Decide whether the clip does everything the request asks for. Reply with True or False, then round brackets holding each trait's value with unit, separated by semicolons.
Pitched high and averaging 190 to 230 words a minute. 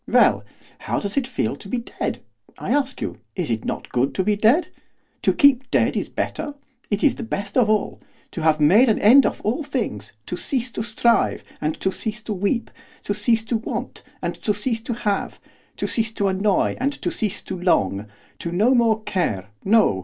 True (215 Hz; 205 wpm)